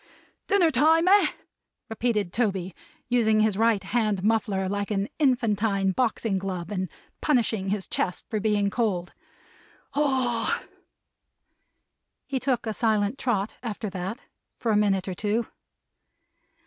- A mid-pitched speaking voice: No, high, 215 Hz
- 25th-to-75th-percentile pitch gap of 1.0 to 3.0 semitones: No, average, 3.5 semitones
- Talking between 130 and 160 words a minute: Yes, slow, 135 wpm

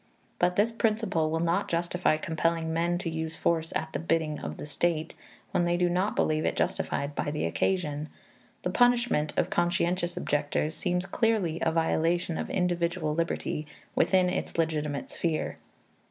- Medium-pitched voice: Yes, medium, 170 Hz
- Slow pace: No, average, 160 wpm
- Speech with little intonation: Yes, narrow, 2.1 semitones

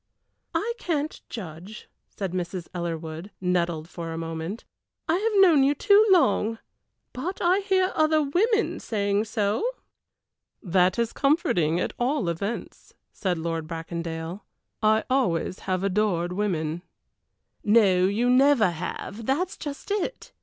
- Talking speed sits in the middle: No, slow, 130 wpm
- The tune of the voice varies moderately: No, wide, 8.7 semitones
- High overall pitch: Yes, high, 205 Hz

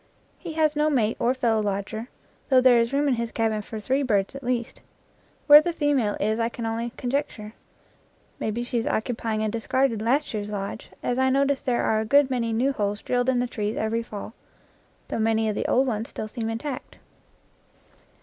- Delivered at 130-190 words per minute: No, fast, 205 wpm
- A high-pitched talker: Yes, high, 235 Hz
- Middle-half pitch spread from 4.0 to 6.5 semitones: No, average, 3.2 semitones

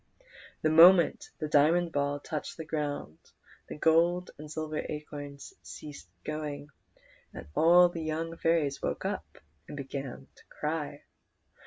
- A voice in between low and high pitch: Yes, medium, 150 Hz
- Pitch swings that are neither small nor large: No, narrow, 2.3 semitones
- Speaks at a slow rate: Yes, slow, 130 wpm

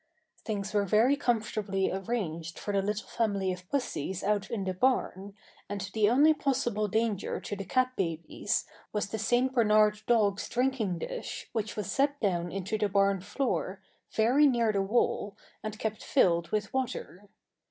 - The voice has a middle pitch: No, high, 210 Hz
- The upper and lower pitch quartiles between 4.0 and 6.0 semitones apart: No, average, 3.5 semitones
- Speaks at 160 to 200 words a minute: Yes, average, 165 wpm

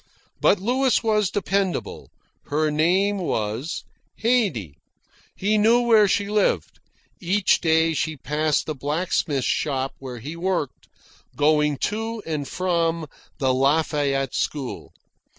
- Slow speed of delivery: Yes, slow, 115 wpm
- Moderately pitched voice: Yes, medium, 165 Hz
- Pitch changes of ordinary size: No, wide, 5.8 semitones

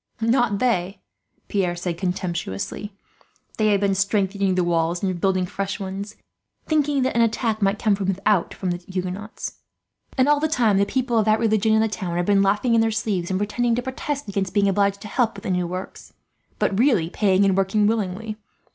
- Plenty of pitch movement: No, average, 3.0 semitones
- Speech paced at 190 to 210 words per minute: Yes, average, 200 wpm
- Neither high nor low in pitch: No, high, 200 Hz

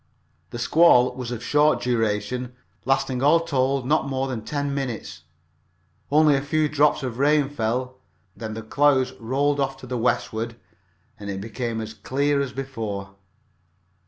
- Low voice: Yes, low, 130 Hz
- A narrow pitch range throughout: No, average, 3.6 semitones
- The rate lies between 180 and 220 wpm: No, average, 155 wpm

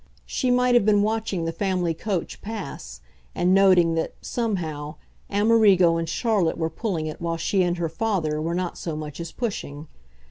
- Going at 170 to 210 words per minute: Yes, average, 175 wpm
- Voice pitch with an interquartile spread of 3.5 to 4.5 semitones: Yes, average, 4.2 semitones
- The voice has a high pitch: No, medium, 175 Hz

